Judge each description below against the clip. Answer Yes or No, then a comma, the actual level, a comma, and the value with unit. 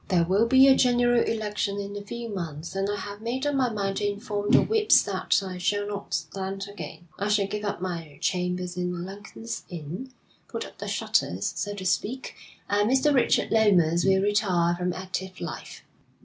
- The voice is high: Yes, high, 200 Hz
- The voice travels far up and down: No, average, 3.2 semitones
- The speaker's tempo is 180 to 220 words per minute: Yes, average, 190 wpm